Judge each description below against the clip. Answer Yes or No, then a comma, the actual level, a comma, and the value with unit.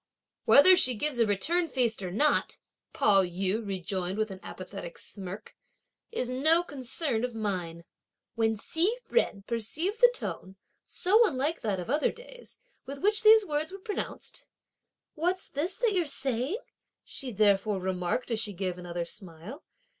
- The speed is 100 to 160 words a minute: Yes, average, 155 wpm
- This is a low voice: No, high, 235 Hz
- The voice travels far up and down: Yes, wide, 9.0 semitones